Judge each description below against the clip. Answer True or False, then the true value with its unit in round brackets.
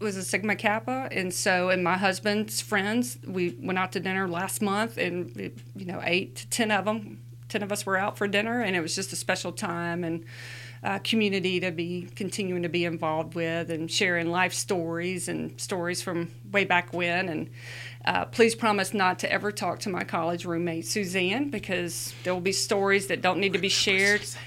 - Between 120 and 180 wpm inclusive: False (205 wpm)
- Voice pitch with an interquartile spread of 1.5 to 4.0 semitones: True (3.1 semitones)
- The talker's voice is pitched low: False (185 Hz)